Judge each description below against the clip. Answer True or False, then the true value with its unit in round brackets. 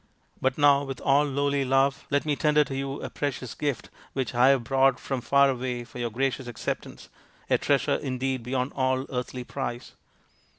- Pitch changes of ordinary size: False (1.7 semitones)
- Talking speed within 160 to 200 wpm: True (180 wpm)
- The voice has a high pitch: False (135 Hz)